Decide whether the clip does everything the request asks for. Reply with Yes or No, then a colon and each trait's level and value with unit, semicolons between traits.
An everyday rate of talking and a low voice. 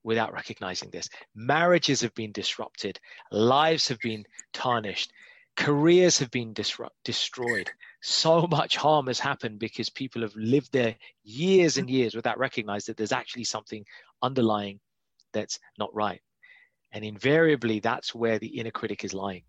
Yes: average, 150 wpm; low, 120 Hz